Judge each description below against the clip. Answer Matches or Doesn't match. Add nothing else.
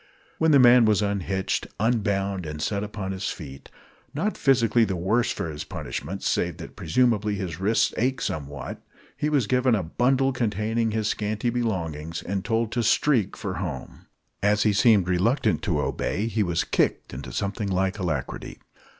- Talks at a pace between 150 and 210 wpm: Matches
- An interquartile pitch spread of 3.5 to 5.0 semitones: Matches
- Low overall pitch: Matches